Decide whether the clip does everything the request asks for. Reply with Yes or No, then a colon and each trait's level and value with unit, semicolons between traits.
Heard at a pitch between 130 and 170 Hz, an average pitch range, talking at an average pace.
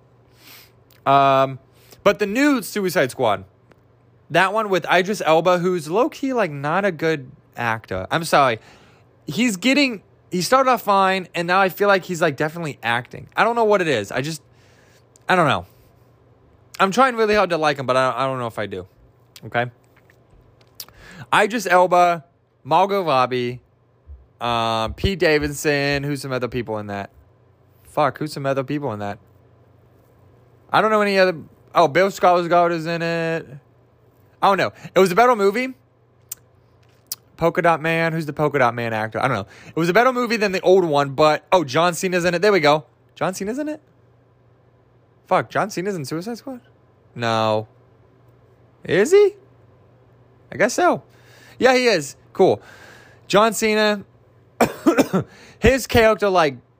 No: medium, 140 Hz; wide, 7.1 semitones; average, 165 wpm